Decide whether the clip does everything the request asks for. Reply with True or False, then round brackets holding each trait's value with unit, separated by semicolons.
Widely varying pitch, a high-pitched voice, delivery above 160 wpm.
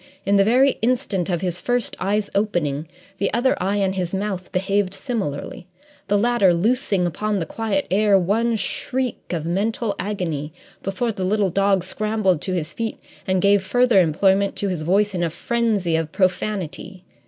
False (3.0 semitones; 195 Hz; 170 wpm)